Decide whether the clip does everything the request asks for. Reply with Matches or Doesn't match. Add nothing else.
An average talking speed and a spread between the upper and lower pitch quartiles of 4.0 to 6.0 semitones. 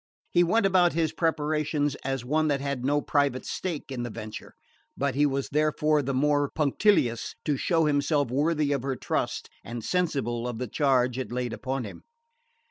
Doesn't match